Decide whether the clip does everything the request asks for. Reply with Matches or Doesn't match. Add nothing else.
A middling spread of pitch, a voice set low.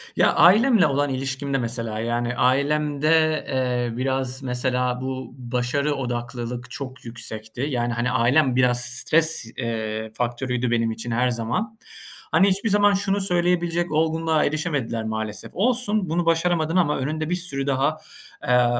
Matches